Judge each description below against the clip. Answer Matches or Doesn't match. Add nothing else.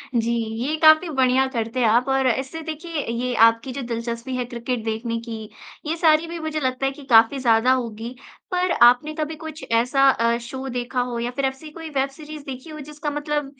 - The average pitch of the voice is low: Doesn't match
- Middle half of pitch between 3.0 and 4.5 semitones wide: Matches